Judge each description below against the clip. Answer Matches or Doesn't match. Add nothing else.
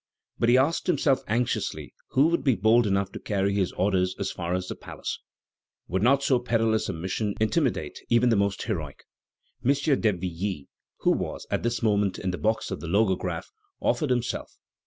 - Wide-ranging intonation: Doesn't match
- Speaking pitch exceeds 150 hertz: Doesn't match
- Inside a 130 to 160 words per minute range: Doesn't match